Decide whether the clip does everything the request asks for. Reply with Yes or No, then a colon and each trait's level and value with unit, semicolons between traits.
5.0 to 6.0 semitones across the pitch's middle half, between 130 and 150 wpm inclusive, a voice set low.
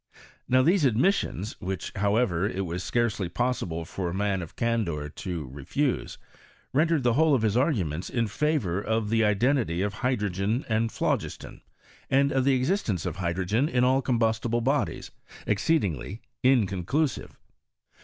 Yes: wide, 5.6 semitones; average, 145 wpm; low, 110 Hz